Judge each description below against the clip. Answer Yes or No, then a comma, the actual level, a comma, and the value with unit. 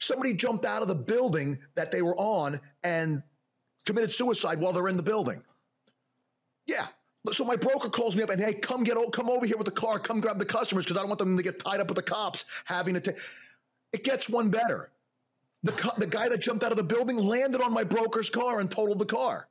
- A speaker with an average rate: No, fast, 235 wpm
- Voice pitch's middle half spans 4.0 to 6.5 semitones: Yes, average, 4.3 semitones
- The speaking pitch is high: Yes, high, 215 Hz